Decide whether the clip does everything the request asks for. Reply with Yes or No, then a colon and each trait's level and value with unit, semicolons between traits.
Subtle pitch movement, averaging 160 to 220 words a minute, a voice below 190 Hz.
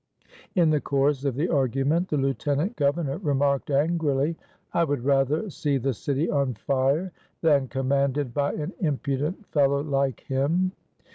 No: narrow, 2.2 semitones; average, 145 wpm; medium, 140 Hz